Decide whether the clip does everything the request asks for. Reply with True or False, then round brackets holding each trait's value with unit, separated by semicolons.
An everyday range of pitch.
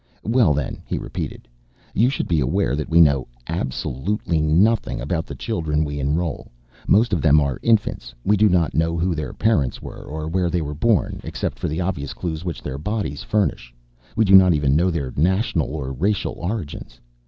True (4.7 semitones)